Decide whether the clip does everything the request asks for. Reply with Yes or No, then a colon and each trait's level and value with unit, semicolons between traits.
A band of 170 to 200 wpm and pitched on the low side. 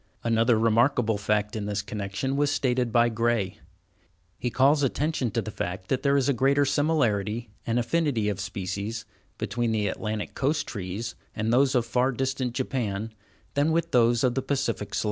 Yes: average, 175 wpm; low, 120 Hz